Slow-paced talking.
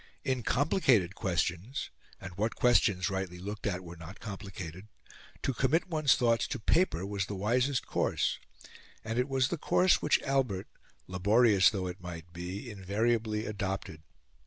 No: average, 150 wpm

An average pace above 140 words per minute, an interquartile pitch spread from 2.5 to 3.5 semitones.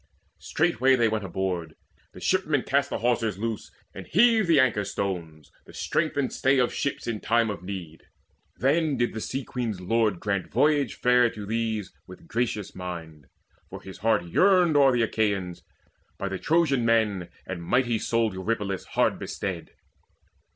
No: average, 165 wpm; average, 5.3 semitones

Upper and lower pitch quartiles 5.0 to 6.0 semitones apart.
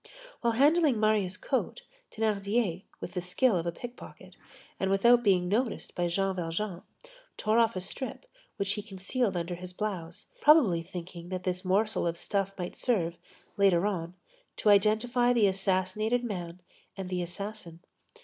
No: average, 3.6 semitones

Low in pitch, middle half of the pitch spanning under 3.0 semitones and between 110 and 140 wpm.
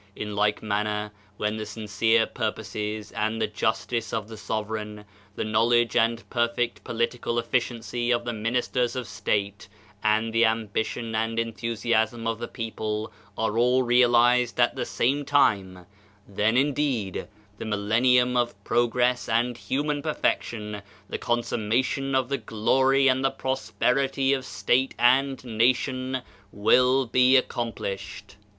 Yes: low, 115 Hz; narrow, 2.6 semitones; slow, 135 wpm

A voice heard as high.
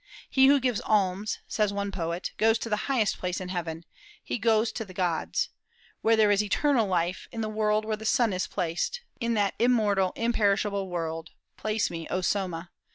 Yes: high, 205 Hz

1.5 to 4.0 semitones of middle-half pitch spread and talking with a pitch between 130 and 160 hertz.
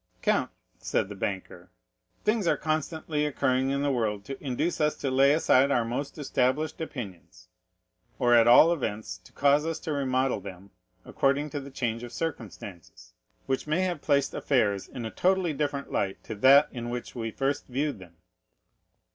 No: average, 4.6 semitones; low, 135 Hz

